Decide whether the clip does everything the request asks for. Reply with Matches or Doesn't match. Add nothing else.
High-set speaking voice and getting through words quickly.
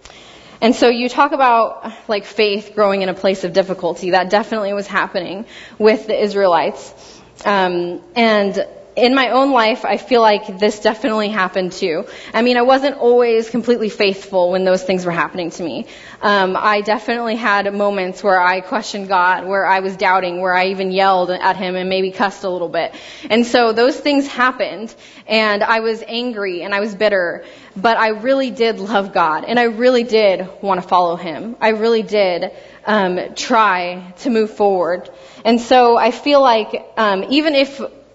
Doesn't match